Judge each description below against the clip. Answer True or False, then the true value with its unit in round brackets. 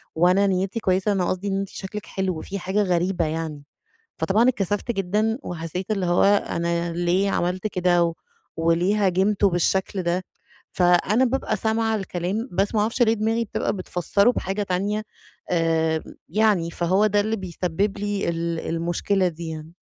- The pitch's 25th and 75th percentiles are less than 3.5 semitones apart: True (3.1 semitones)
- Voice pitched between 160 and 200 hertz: True (190 Hz)